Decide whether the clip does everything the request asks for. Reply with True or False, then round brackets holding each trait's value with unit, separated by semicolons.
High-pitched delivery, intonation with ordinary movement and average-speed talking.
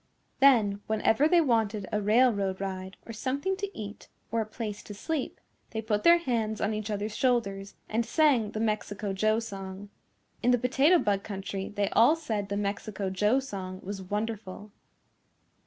True (215 Hz; 3.2 semitones; 170 wpm)